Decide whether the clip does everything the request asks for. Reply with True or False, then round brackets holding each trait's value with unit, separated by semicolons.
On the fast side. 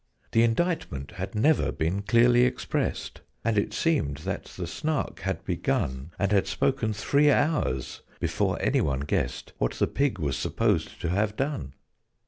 False (155 wpm)